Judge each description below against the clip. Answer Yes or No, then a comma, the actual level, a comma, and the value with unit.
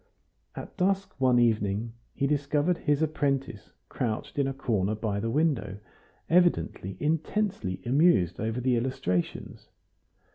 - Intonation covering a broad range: Yes, wide, 6.0 semitones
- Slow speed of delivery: Yes, slow, 120 wpm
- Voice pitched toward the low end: Yes, low, 130 Hz